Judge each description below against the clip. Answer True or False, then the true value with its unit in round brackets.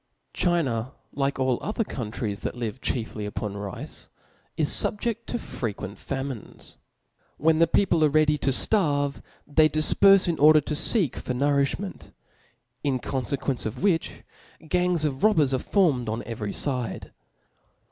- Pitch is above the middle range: False (140 Hz)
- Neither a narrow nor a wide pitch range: True (4.8 semitones)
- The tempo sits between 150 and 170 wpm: False (140 wpm)